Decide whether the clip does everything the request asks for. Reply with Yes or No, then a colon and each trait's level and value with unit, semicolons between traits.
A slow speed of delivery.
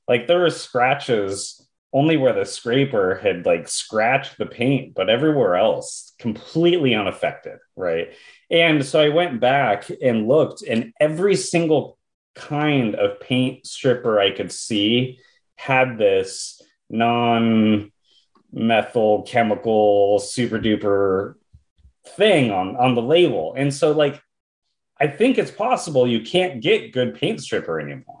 Yes: slow, 130 wpm